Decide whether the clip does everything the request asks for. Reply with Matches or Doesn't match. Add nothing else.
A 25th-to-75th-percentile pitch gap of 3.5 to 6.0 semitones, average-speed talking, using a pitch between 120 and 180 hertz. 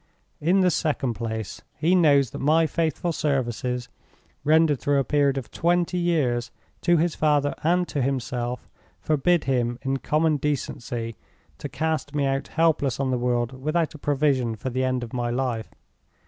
Matches